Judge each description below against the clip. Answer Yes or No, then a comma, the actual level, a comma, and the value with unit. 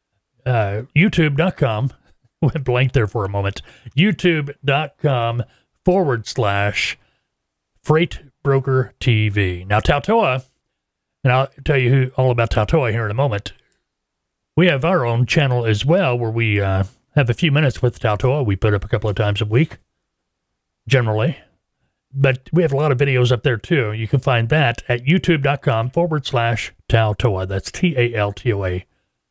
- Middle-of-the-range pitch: No, low, 125 Hz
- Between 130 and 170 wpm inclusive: Yes, average, 165 wpm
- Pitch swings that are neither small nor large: Yes, average, 4.9 semitones